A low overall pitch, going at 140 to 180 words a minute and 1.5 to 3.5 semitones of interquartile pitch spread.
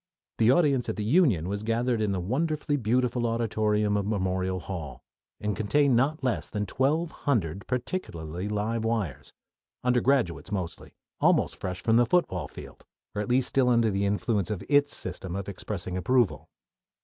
No: low, 110 Hz; average, 160 wpm; average, 4.6 semitones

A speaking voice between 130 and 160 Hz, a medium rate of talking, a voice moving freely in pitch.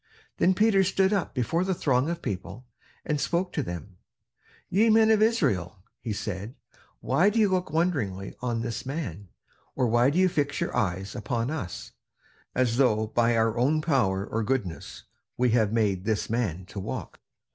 No: low, 120 Hz; average, 175 wpm; wide, 8.3 semitones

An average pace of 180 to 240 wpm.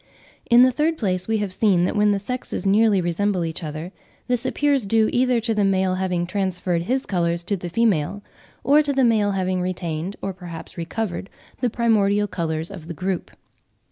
Yes: average, 190 wpm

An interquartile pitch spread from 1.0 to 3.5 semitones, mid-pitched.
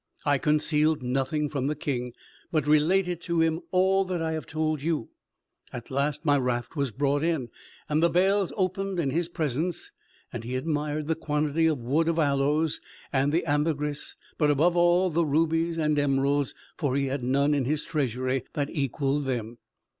Yes: average, 2.8 semitones; medium, 150 Hz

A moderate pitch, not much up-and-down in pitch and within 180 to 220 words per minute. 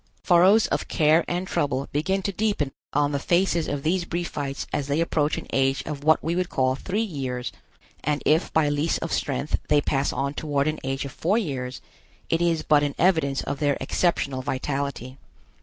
No: medium, 150 Hz; average, 3.6 semitones; average, 190 wpm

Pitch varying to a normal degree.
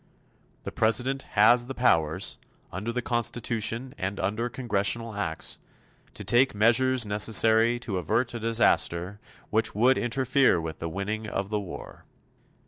Yes: average, 3.0 semitones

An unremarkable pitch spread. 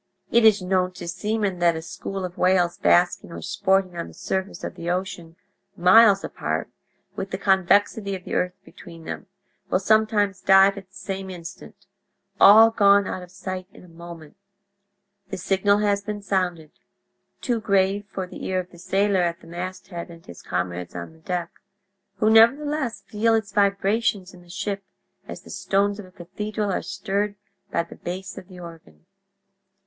No: narrow, 2.3 semitones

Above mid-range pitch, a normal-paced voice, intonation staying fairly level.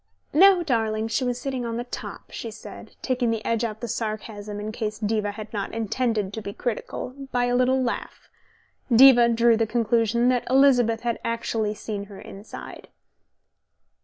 Yes: high, 230 Hz; average, 170 wpm; narrow, 2.3 semitones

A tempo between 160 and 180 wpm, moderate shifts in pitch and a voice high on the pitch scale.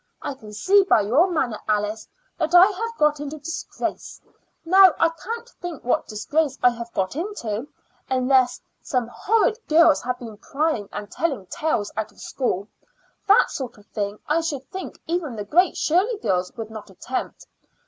No: average, 170 wpm; wide, 7.5 semitones; very high, 275 Hz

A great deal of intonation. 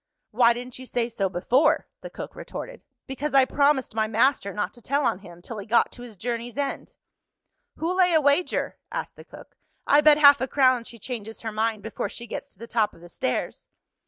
No: average, 4.4 semitones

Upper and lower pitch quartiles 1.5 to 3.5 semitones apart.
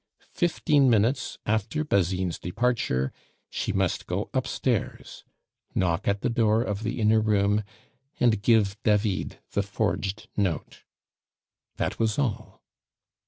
Yes: narrow, 2.6 semitones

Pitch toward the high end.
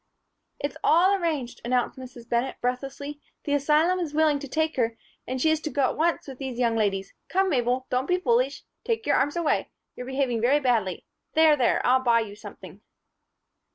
Yes: very high, 265 Hz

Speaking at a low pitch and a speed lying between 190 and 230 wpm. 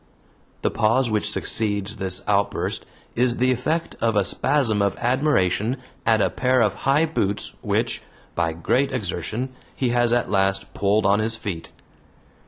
No: low, 110 Hz; average, 155 wpm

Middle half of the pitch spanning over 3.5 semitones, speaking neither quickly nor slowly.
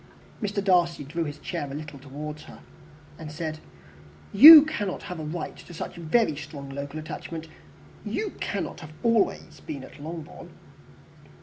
Yes: average, 3.9 semitones; average, 150 wpm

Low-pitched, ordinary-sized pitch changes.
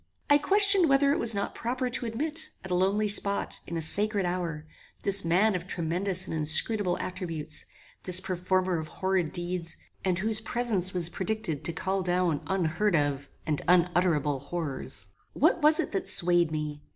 No: medium, 185 Hz; average, 4.0 semitones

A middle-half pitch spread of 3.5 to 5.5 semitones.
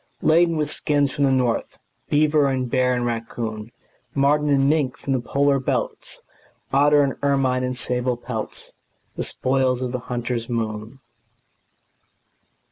No: narrow, 2.6 semitones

